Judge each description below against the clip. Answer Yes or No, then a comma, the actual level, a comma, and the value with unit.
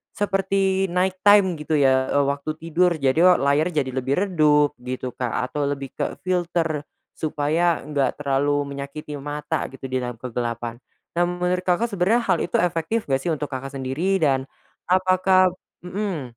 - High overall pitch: No, medium, 150 Hz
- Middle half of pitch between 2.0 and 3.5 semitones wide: No, average, 4.8 semitones